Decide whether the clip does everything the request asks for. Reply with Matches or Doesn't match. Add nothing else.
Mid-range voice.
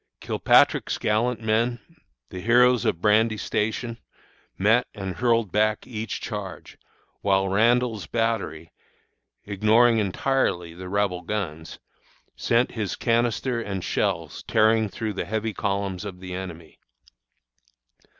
Doesn't match